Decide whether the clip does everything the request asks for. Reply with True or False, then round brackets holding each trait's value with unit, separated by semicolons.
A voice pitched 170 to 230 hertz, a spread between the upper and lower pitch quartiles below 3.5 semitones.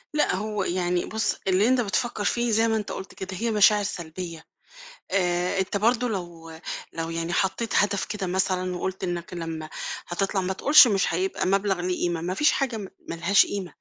True (190 Hz; 3.0 semitones)